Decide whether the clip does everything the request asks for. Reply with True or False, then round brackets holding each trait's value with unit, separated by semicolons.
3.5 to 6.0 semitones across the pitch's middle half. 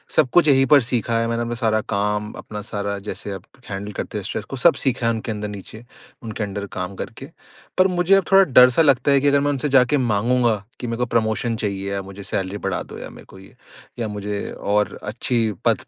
True (3.9 semitones)